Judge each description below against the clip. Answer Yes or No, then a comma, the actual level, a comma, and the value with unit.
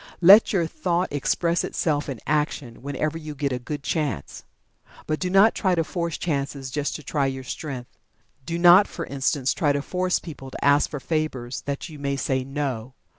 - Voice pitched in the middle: Yes, medium, 145 Hz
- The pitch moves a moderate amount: Yes, average, 3.6 semitones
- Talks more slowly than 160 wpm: No, average, 190 wpm